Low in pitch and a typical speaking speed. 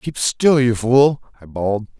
Yes: low, 125 Hz; average, 180 wpm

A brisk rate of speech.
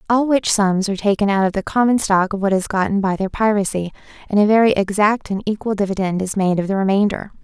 Yes: fast, 235 wpm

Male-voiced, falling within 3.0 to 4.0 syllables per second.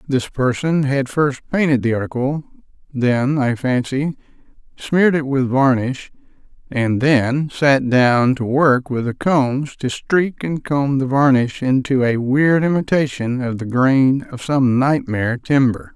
Yes: male; 3.9 syllables/s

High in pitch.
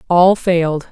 No: medium, 175 Hz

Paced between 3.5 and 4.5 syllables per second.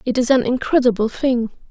No: 5.5 syllables/s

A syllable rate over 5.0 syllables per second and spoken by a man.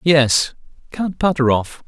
No: 3.6 syllables/s; male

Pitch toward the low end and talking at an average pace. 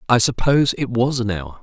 No: low, 120 Hz; fast, 220 wpm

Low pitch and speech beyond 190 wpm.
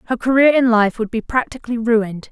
No: high, 235 Hz; fast, 205 wpm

